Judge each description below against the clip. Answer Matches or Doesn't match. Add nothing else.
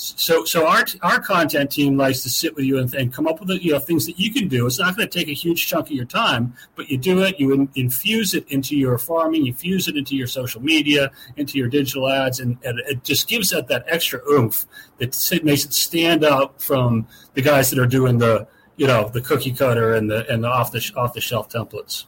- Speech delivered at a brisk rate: Matches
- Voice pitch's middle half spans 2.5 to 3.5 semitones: Doesn't match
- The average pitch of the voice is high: Doesn't match